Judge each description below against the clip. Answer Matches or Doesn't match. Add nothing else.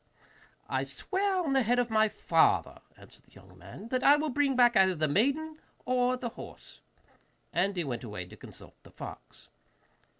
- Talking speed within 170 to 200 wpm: Matches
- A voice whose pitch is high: Matches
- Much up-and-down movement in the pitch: Matches